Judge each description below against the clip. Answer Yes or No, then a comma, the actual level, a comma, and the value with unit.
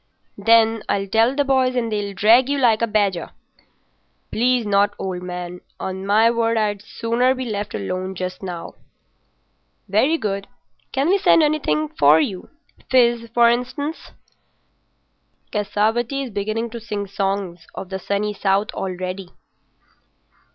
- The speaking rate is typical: Yes, average, 145 wpm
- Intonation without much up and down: No, average, 3.6 semitones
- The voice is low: No, high, 210 Hz